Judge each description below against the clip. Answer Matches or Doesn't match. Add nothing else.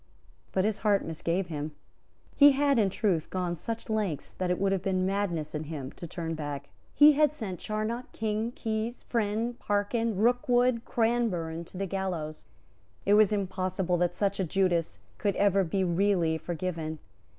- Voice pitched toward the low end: Doesn't match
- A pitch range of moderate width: Matches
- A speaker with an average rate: Matches